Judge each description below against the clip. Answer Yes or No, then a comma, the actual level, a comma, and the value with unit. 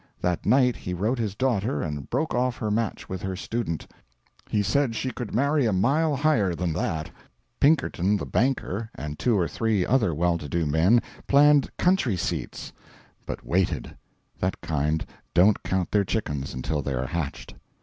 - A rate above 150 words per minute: Yes, average, 170 wpm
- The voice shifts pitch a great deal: Yes, wide, 6.8 semitones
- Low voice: Yes, low, 105 Hz